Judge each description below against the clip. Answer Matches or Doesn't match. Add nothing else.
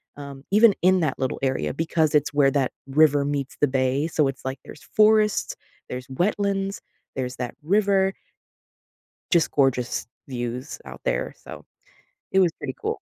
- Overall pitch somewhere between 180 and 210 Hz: Doesn't match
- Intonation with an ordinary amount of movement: Doesn't match